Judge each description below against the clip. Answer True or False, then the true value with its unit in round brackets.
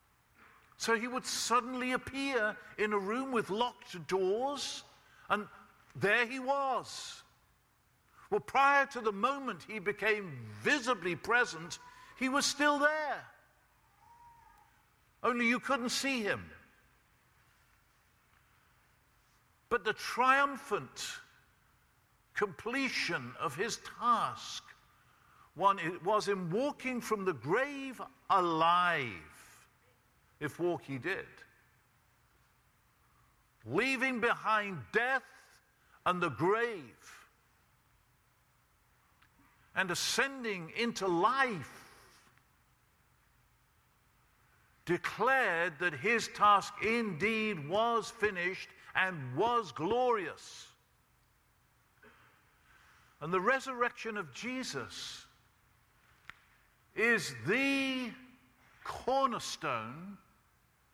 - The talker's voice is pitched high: True (230 Hz)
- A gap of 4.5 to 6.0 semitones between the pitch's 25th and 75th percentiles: True (5.3 semitones)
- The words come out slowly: True (80 wpm)